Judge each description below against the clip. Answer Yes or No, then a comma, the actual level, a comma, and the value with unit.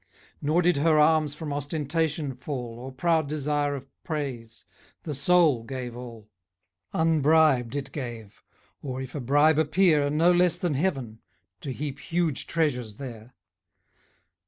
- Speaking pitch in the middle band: Yes, medium, 145 Hz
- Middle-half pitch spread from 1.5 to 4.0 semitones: Yes, average, 3.7 semitones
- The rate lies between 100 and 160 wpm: Yes, slow, 135 wpm